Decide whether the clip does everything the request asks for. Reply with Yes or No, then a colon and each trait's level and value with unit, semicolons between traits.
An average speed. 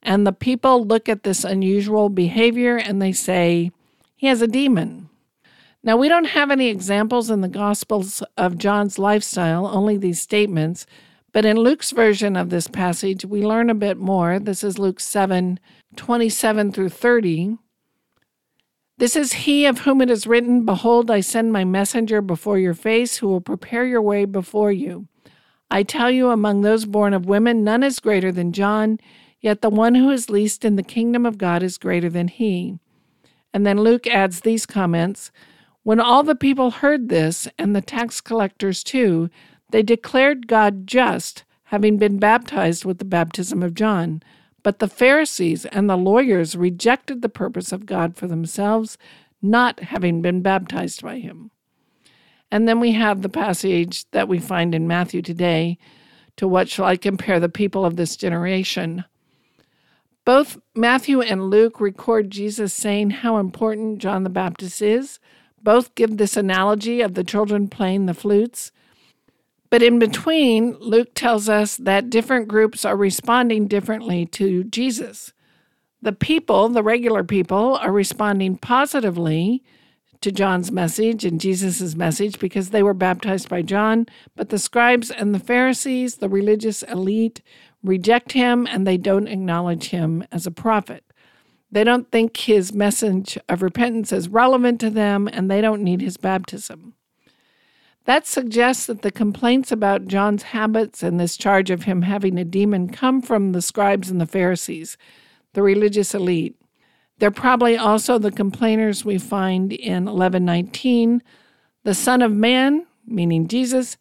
Yes: average, 160 wpm